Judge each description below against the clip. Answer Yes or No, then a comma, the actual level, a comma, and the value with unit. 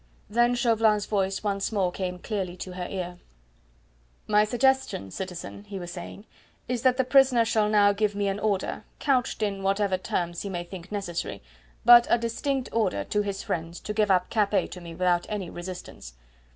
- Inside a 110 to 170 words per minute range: No, average, 180 wpm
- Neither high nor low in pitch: No, high, 200 Hz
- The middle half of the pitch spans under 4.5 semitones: Yes, average, 3.4 semitones